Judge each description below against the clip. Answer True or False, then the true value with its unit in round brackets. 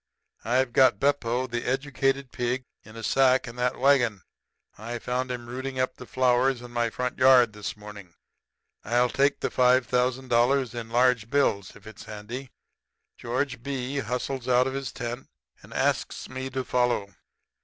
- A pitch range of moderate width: False (1.9 semitones)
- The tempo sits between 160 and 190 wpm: True (165 wpm)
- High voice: False (125 Hz)